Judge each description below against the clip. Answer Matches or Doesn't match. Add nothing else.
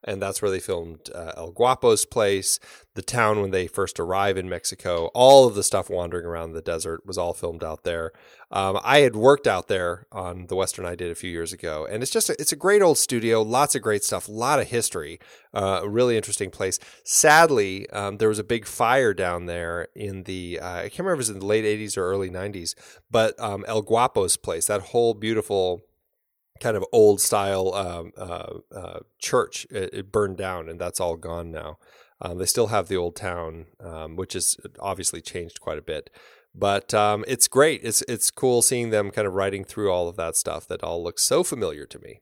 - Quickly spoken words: Matches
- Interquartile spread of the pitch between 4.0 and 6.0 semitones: Matches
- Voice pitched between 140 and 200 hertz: Doesn't match